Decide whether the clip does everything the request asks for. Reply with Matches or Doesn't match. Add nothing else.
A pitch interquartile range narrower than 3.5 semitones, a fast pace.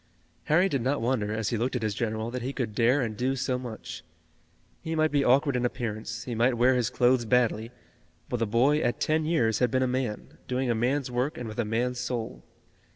Matches